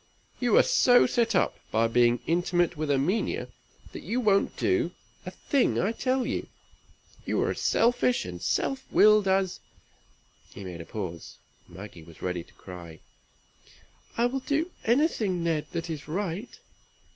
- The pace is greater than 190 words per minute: No, average, 155 wpm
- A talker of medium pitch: Yes, medium, 180 Hz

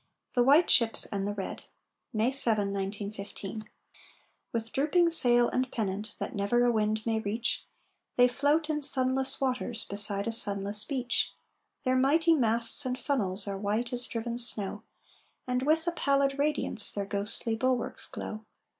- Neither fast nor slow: Yes, average, 155 wpm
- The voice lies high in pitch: Yes, high, 235 Hz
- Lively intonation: No, average, 4.3 semitones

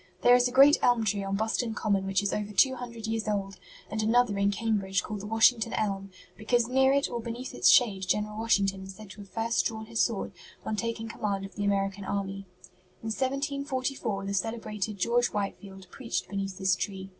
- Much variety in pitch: No, average, 3.0 semitones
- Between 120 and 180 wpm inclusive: No, average, 200 wpm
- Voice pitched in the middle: No, high, 215 Hz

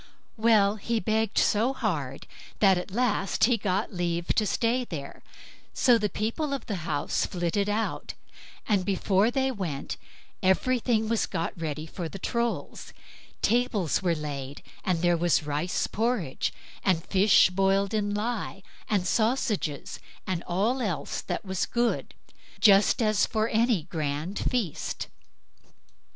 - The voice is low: No, high, 200 Hz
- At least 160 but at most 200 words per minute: No, average, 140 wpm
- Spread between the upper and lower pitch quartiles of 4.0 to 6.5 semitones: Yes, average, 4.5 semitones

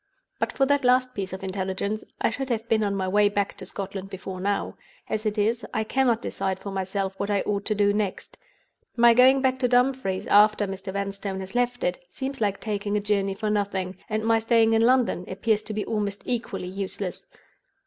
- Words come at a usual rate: No, fast, 210 wpm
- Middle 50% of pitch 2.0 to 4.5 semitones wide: Yes, average, 2.9 semitones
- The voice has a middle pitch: No, high, 205 Hz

